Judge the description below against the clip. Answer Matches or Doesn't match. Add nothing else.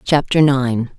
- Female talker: Matches